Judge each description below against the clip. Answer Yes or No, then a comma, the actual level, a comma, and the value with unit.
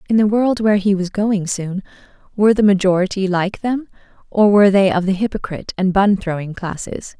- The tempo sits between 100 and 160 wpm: No, average, 190 wpm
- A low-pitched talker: No, high, 195 Hz